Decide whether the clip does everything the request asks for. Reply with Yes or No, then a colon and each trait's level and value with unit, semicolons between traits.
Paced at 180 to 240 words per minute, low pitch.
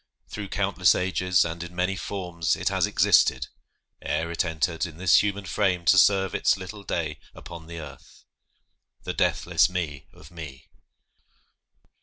No: average, 150 wpm; very low, 90 Hz